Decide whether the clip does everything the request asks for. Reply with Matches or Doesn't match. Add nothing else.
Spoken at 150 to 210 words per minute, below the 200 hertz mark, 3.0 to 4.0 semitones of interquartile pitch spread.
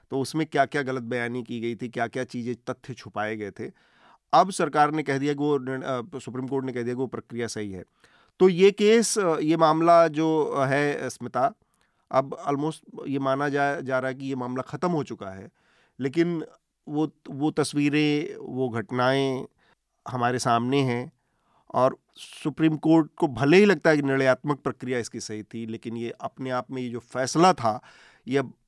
Matches